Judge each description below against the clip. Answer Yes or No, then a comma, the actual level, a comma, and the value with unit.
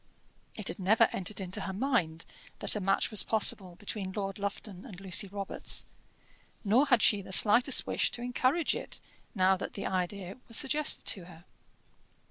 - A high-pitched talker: Yes, high, 200 Hz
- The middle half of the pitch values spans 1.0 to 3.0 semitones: No, average, 3.5 semitones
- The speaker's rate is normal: Yes, average, 170 wpm